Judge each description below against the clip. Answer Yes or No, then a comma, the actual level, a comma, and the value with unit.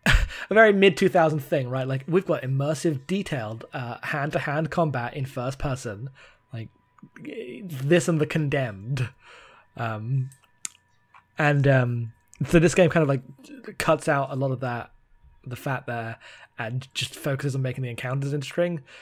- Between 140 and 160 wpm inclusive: Yes, average, 155 wpm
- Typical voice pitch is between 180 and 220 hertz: No, low, 135 Hz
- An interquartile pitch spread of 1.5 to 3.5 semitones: No, average, 4.3 semitones